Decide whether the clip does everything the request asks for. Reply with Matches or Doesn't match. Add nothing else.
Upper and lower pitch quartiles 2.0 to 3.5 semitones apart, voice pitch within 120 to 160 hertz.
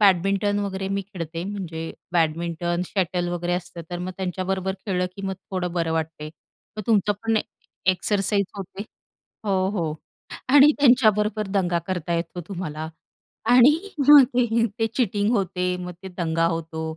Doesn't match